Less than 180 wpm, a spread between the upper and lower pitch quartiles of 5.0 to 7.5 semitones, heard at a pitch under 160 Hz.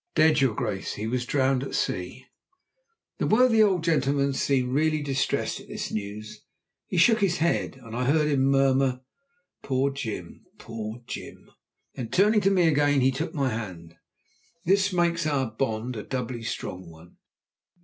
Yes: average, 160 wpm; wide, 5.4 semitones; low, 135 Hz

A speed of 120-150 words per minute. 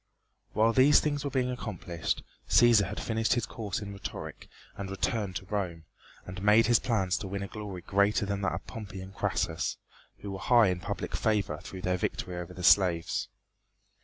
No: average, 190 wpm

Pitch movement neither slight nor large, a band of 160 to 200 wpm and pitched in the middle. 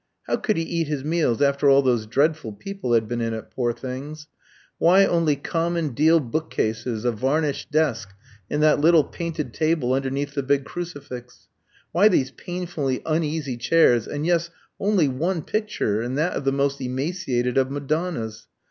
Yes: average, 4.5 semitones; average, 170 wpm; medium, 145 Hz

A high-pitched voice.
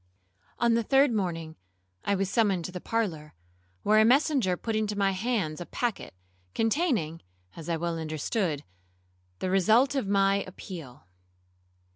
Yes: high, 195 Hz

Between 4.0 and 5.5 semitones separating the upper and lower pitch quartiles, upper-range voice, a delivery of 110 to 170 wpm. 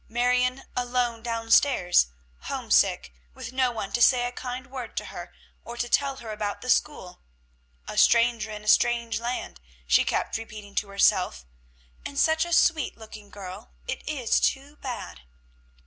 No: average, 3.0 semitones; high, 240 Hz; average, 160 wpm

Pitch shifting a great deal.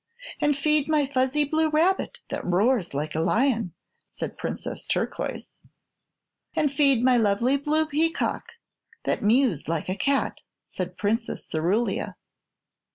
Yes: wide, 6.3 semitones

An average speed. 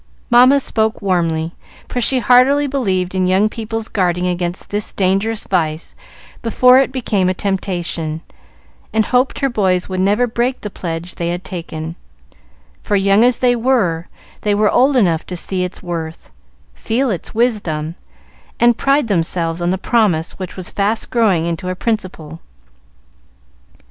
Yes: average, 155 wpm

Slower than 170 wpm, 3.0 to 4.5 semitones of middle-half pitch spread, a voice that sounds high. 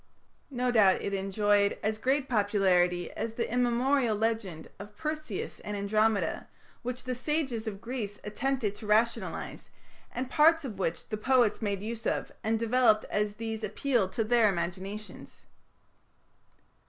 Yes: average, 140 wpm; average, 3.3 semitones; high, 220 Hz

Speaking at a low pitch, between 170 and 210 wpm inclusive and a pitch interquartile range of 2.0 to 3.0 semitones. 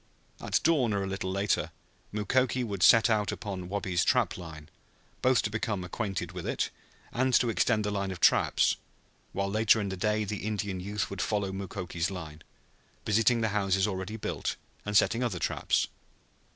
Yes: low, 100 Hz; average, 175 wpm; narrow, 2.5 semitones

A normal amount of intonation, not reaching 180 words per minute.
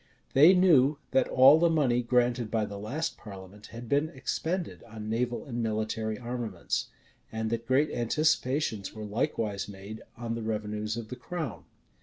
Yes: average, 4.0 semitones; average, 160 wpm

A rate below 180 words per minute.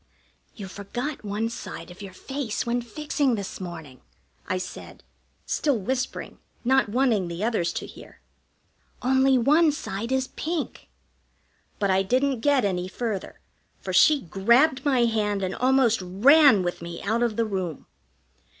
Yes: average, 150 wpm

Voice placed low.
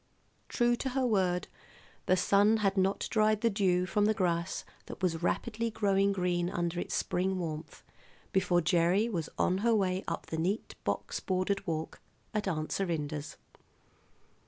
No: medium, 185 Hz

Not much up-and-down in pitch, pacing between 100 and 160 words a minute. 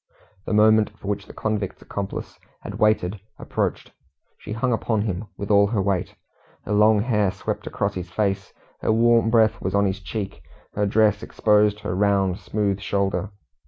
No: narrow, 1.6 semitones; average, 170 wpm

